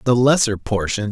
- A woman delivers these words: No, male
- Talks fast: No, average, 160 wpm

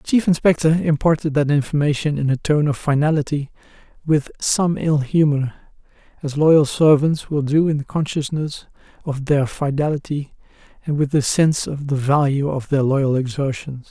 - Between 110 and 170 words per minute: Yes, average, 160 wpm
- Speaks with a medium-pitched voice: Yes, medium, 145 Hz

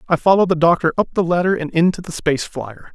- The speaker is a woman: No, male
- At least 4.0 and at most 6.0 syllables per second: No, 6.8 syllables/s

